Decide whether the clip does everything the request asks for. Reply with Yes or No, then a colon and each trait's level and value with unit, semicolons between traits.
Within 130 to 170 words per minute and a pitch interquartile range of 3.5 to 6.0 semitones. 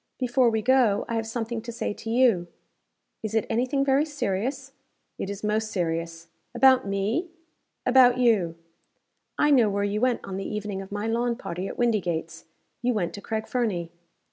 No: average, 180 wpm; average, 4.0 semitones